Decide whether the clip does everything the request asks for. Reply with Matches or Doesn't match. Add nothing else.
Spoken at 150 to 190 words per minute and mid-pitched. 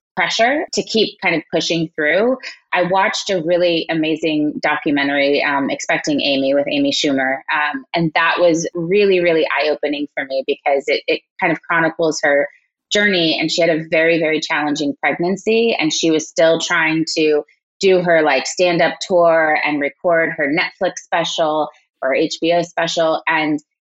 Matches